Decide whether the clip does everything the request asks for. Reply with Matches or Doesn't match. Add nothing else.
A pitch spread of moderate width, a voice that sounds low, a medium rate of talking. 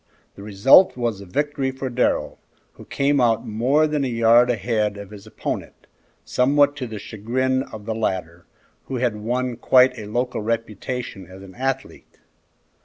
Matches